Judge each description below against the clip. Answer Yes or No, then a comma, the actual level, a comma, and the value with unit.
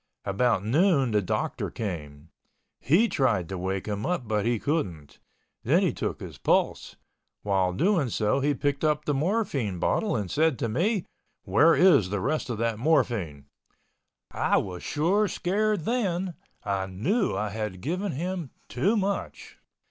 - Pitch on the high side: No, low, 130 Hz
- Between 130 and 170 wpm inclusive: Yes, average, 155 wpm